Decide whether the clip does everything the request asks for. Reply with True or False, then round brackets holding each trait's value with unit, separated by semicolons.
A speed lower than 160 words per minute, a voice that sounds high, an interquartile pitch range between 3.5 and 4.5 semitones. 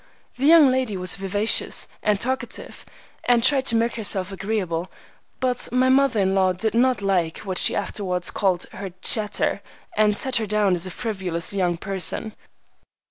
False (165 wpm; 205 Hz; 4.1 semitones)